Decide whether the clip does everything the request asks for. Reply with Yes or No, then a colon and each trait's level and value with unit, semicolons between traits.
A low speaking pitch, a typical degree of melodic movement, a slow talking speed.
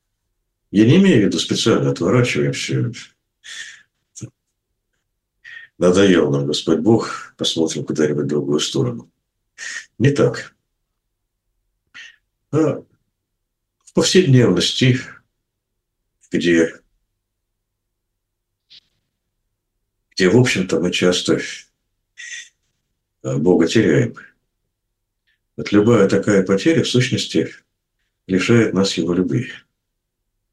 Yes: low, 105 Hz; average, 4.6 semitones; slow, 75 wpm